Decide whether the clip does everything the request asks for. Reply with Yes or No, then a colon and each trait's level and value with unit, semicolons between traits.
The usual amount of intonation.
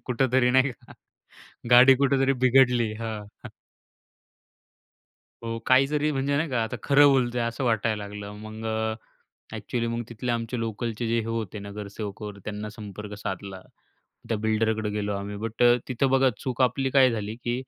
Yes: average, 3.3 semitones